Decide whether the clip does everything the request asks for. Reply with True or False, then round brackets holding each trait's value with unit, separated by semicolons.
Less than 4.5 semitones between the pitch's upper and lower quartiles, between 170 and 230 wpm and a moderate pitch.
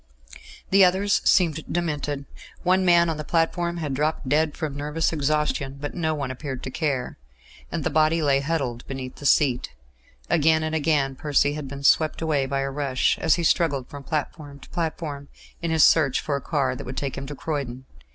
True (2.7 semitones; 195 wpm; 150 Hz)